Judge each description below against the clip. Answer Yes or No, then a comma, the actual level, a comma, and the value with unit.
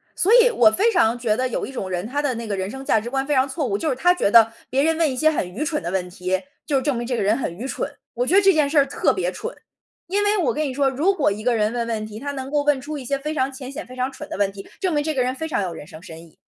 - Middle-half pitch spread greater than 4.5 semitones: Yes, wide, 5.6 semitones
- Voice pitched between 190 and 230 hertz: No, very high, 260 Hz